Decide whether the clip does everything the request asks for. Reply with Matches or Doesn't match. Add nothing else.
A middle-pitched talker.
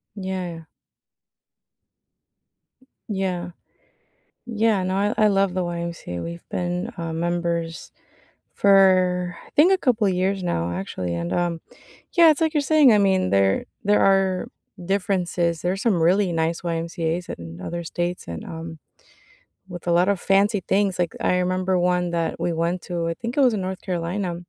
Matches